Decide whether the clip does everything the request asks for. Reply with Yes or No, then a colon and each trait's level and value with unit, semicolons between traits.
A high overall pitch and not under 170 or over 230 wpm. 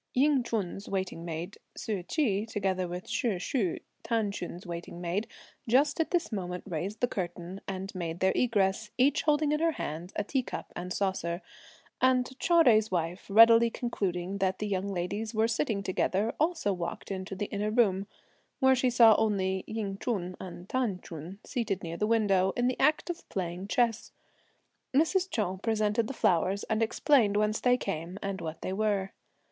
Yes: high, 200 Hz; average, 175 wpm